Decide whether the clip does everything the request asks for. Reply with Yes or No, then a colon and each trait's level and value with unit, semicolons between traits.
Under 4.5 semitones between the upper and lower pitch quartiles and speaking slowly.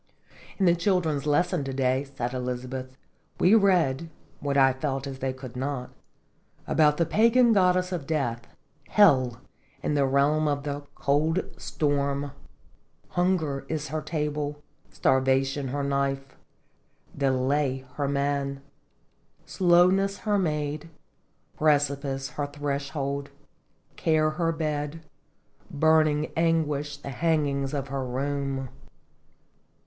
Yes: narrow, 2.6 semitones; slow, 125 wpm